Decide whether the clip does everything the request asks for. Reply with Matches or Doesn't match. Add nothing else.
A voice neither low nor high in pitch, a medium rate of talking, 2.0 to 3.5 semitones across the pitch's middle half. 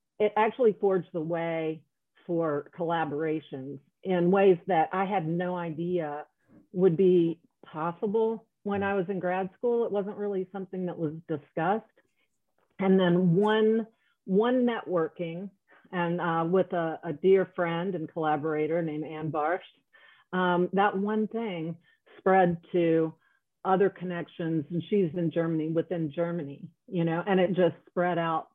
Matches